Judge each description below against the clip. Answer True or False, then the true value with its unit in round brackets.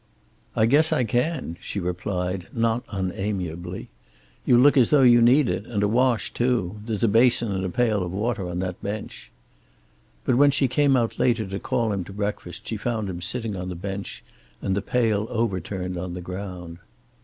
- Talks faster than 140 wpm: True (190 wpm)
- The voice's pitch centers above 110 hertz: False (105 Hz)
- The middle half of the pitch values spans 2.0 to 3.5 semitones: False (4.7 semitones)